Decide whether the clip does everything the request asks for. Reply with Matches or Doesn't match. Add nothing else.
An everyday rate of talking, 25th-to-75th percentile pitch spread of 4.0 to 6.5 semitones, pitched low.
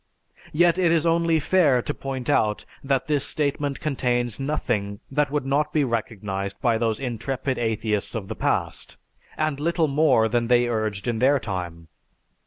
Matches